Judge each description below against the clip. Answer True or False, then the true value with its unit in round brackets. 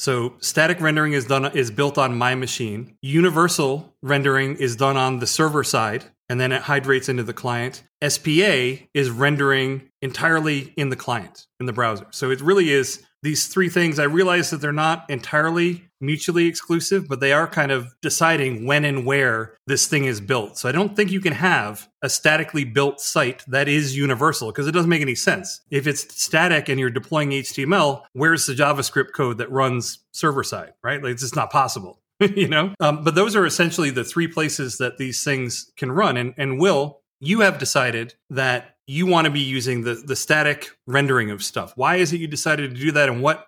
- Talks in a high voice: False (140 Hz)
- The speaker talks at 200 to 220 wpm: True (205 wpm)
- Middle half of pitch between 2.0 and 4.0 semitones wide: True (3.3 semitones)